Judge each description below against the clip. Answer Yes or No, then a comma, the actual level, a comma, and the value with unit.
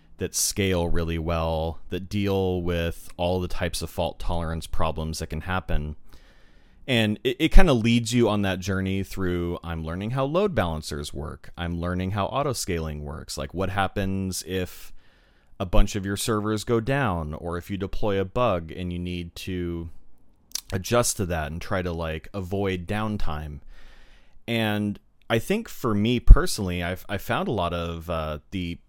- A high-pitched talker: No, very low, 90 Hz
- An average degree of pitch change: Yes, average, 3.6 semitones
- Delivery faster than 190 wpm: No, average, 175 wpm